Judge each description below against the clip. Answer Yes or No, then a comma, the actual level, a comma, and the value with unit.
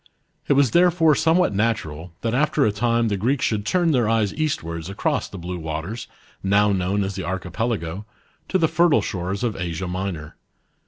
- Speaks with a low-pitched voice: Yes, low, 105 Hz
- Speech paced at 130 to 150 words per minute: No, average, 180 wpm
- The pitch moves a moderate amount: No, wide, 6.0 semitones